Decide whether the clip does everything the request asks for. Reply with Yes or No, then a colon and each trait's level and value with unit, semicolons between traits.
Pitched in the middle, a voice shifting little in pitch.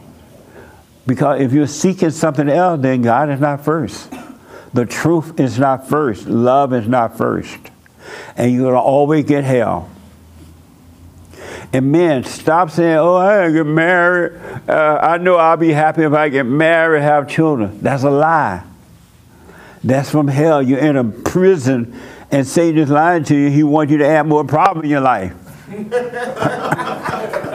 No: medium, 145 Hz; average, 3.9 semitones